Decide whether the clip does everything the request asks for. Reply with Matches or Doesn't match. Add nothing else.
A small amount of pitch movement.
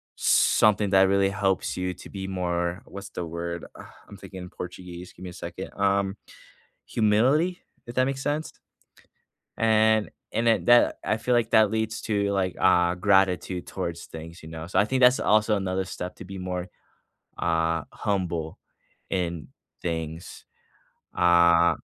Doesn't match